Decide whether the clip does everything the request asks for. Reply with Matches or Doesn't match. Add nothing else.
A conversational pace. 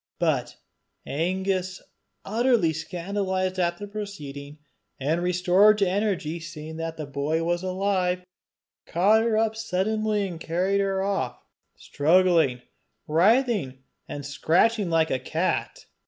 Doesn't match